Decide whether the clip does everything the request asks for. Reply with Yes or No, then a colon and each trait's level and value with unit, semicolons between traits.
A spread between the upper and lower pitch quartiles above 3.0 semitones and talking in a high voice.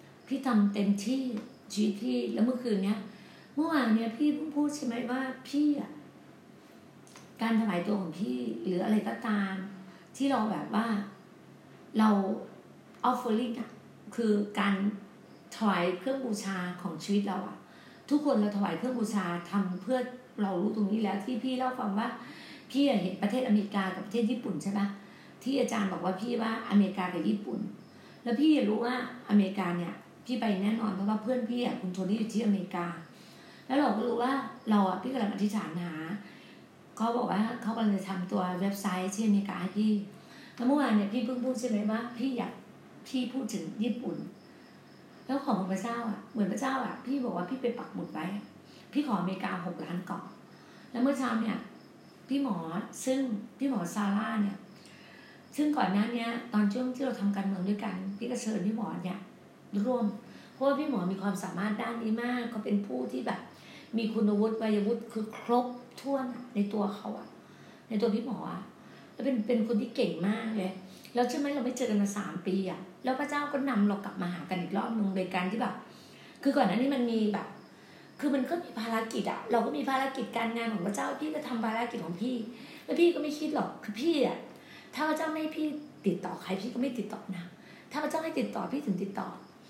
Yes: average, 4.0 semitones; high, 220 Hz